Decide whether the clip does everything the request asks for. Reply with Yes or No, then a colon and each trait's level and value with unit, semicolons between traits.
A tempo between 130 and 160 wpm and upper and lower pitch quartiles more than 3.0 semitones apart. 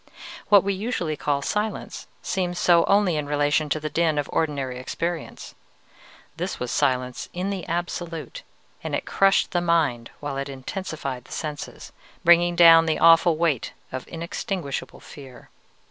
Yes: average, 150 wpm; average, 3.6 semitones